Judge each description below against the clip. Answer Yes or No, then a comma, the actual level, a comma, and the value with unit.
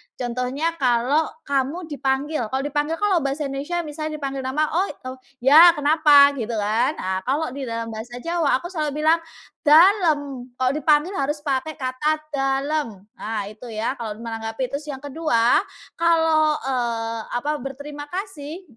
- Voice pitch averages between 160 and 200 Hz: No, very high, 280 Hz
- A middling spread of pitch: Yes, average, 3.8 semitones